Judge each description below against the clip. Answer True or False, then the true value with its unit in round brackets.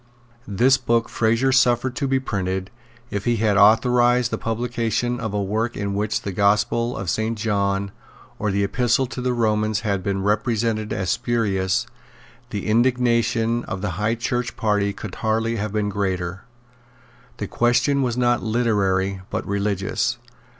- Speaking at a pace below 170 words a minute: True (155 wpm)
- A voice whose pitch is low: True (110 Hz)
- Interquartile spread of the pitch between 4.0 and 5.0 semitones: False (3.0 semitones)